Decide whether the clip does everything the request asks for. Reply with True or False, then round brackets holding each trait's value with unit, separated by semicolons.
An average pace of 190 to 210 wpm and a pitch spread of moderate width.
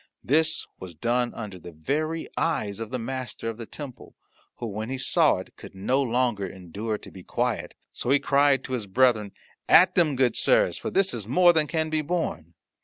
False (200 wpm; 6.3 semitones)